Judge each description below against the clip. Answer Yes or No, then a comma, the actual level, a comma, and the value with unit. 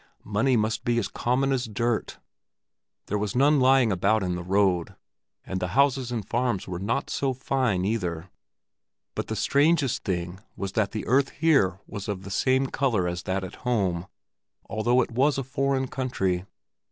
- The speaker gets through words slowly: No, average, 175 wpm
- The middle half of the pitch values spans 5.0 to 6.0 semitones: Yes, wide, 5.6 semitones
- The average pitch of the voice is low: Yes, low, 110 Hz